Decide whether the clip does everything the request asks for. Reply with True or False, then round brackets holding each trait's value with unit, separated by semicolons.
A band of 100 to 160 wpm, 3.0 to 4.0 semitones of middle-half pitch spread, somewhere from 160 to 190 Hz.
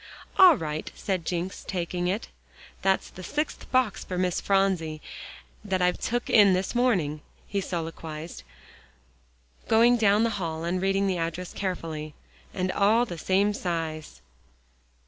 True (140 wpm; 3.5 semitones; 185 Hz)